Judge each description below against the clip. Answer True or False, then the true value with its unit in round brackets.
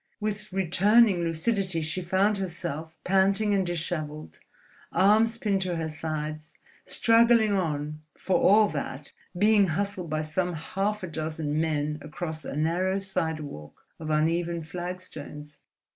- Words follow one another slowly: True (130 wpm)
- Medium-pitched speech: True (175 Hz)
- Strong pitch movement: False (4.0 semitones)